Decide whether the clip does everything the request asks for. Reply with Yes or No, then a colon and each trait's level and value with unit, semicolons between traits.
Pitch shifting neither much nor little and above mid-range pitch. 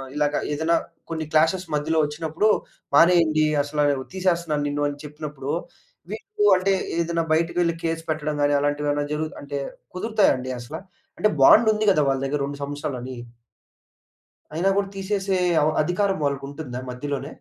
No: average, 3.1 semitones; medium, 155 Hz